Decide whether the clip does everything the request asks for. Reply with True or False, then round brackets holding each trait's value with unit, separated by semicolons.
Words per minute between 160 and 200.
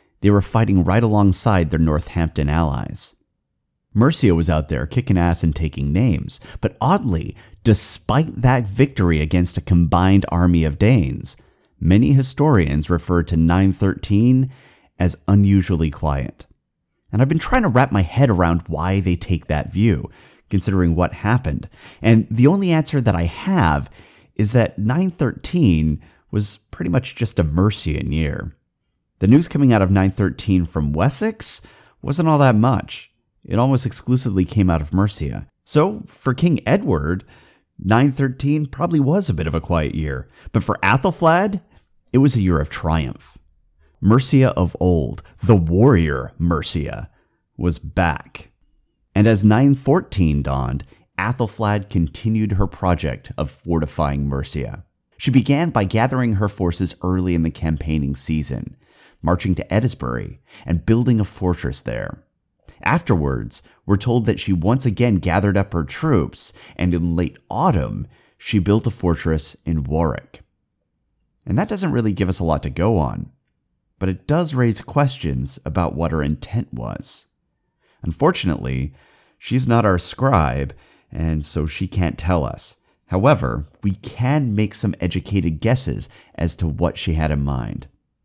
False (145 wpm)